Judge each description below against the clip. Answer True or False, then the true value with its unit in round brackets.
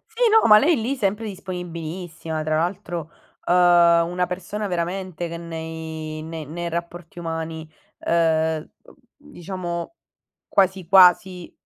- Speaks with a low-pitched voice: False (175 Hz)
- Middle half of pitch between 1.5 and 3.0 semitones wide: True (2.5 semitones)